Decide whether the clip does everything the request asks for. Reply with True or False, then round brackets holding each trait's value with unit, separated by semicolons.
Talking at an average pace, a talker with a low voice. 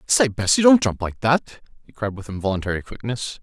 False (210 wpm; 115 Hz)